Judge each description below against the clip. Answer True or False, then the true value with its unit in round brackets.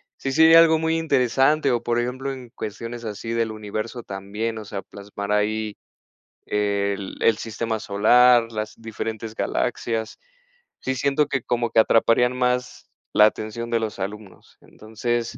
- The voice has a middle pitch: False (115 Hz)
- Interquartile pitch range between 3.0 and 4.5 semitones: False (2.6 semitones)